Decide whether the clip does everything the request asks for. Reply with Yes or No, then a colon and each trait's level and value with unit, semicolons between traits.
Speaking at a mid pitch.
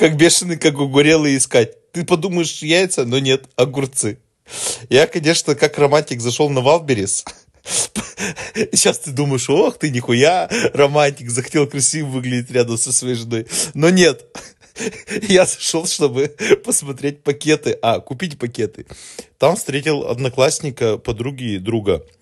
Yes: medium, 145 Hz